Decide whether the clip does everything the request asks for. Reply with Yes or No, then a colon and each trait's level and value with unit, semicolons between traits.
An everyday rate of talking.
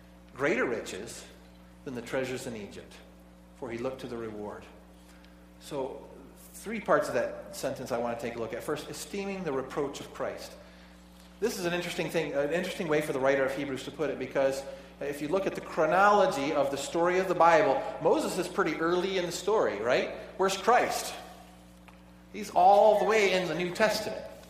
Yes: average, 195 wpm